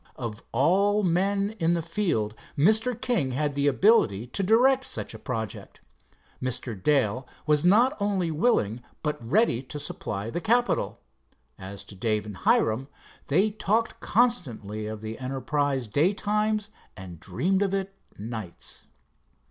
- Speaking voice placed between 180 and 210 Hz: No, medium, 150 Hz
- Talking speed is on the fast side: No, average, 140 wpm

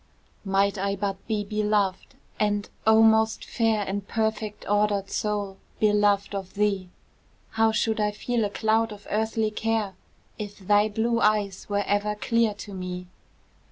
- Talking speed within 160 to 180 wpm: No, average, 150 wpm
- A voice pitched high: Yes, high, 210 Hz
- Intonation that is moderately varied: No, narrow, 1.5 semitones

